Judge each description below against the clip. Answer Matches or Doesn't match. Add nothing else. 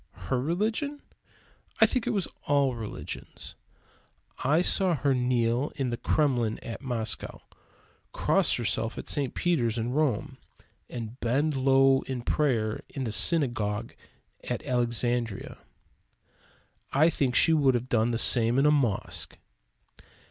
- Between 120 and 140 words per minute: Matches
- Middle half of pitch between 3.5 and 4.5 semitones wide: Matches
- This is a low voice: Matches